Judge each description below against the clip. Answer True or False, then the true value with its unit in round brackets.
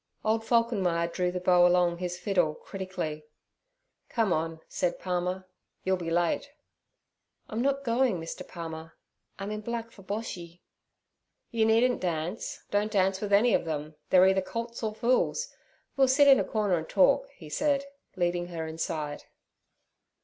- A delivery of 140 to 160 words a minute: True (155 wpm)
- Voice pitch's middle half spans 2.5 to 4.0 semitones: False (4.7 semitones)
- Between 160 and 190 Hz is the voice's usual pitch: True (185 Hz)